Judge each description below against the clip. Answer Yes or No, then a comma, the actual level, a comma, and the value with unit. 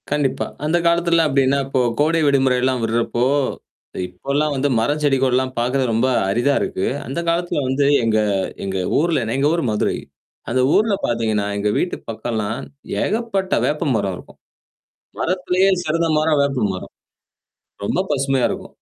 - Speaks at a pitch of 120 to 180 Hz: Yes, low, 135 Hz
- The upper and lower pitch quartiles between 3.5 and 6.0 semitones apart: Yes, average, 4.9 semitones